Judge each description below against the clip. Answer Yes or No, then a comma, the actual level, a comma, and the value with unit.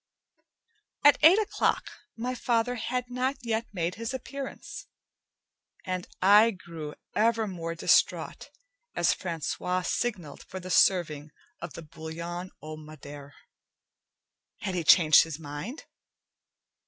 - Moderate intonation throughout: No, wide, 6.3 semitones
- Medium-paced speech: No, slow, 115 wpm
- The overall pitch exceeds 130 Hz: Yes, medium, 185 Hz